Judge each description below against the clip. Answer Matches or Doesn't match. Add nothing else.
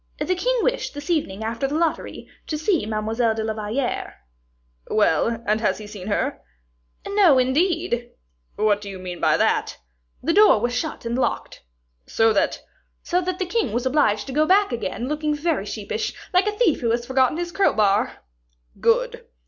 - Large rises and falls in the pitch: Matches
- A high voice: Matches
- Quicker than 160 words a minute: Matches